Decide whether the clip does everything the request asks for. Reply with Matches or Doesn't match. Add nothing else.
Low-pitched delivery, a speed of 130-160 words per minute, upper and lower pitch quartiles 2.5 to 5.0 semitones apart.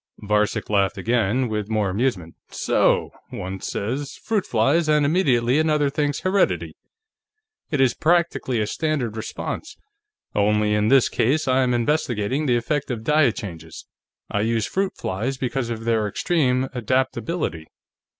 Doesn't match